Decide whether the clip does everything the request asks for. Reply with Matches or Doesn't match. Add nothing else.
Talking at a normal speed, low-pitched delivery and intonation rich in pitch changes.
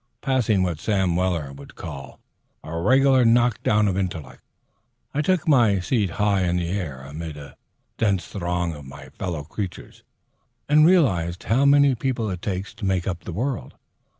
Matches